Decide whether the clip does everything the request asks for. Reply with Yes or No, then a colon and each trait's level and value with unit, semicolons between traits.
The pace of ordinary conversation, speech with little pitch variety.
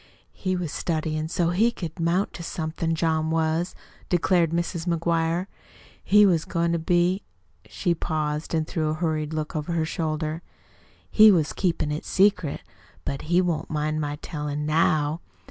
Yes: average, 160 wpm; narrow, 2.0 semitones